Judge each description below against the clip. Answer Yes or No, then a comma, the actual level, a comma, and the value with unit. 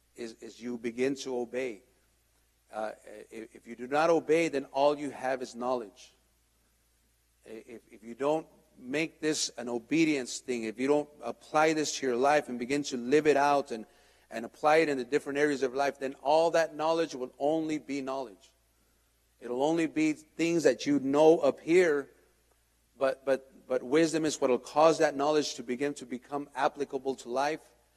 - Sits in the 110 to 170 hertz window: Yes, medium, 140 Hz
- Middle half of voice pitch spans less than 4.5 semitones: Yes, average, 3.7 semitones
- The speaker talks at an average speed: Yes, average, 185 wpm